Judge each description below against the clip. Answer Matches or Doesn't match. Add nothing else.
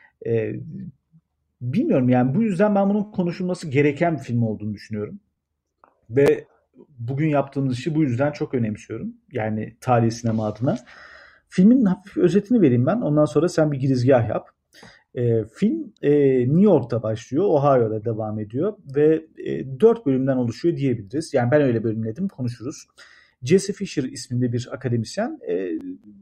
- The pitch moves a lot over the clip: Matches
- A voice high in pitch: Doesn't match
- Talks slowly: Doesn't match